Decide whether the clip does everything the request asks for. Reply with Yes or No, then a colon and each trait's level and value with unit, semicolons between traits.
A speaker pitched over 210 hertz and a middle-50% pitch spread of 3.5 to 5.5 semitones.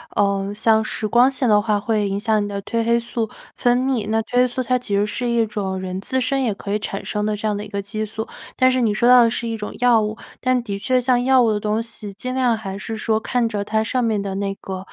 No: high, 220 Hz; average, 2.9 semitones